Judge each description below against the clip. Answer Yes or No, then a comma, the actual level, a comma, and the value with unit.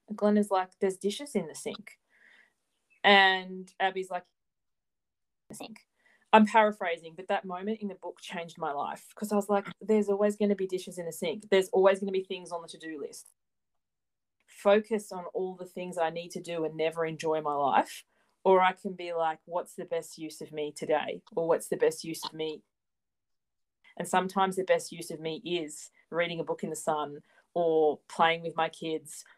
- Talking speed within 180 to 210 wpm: Yes, fast, 205 wpm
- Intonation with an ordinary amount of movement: Yes, average, 3.6 semitones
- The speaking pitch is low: No, medium, 180 Hz